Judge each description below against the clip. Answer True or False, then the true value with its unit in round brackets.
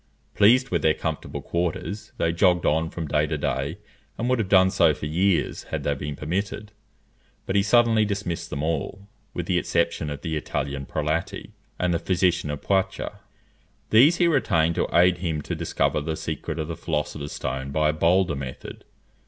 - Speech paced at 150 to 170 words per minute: False (185 wpm)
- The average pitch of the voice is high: False (85 Hz)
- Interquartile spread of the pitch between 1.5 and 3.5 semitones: False (4.2 semitones)